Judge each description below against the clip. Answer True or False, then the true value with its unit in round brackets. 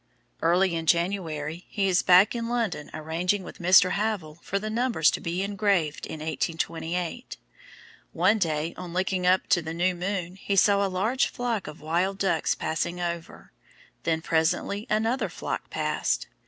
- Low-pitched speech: False (180 Hz)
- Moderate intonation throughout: True (3.4 semitones)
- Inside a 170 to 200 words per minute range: False (160 wpm)